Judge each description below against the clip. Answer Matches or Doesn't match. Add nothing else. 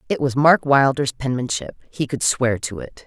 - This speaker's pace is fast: Doesn't match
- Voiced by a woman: Matches